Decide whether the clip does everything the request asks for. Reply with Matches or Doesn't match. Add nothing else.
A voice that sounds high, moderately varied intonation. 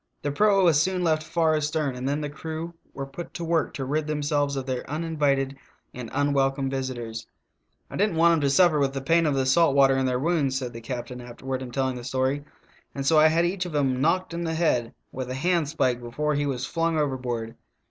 Doesn't match